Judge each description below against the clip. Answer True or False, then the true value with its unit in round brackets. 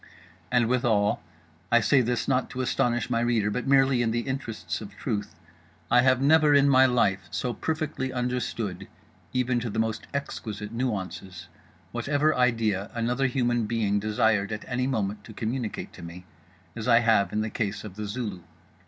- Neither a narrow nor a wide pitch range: True (3.3 semitones)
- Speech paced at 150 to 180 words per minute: True (165 wpm)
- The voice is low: True (115 Hz)